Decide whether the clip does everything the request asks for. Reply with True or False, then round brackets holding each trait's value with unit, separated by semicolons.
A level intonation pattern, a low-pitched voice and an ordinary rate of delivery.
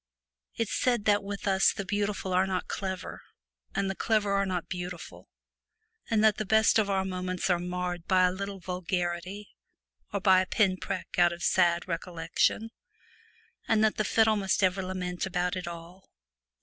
False (2.2 semitones; 190 Hz; 175 wpm)